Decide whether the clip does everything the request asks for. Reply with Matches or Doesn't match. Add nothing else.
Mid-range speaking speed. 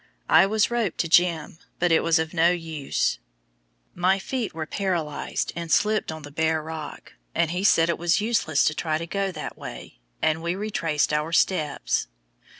Matches